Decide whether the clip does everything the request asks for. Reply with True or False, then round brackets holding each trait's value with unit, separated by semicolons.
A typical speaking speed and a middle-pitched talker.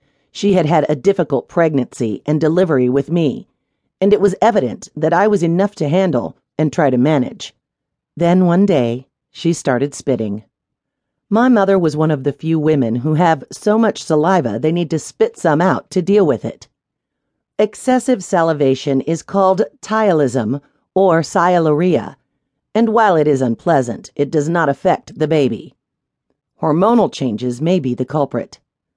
True (160 wpm; 155 Hz)